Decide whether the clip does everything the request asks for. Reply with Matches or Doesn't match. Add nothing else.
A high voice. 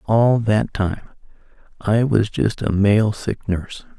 Doesn't match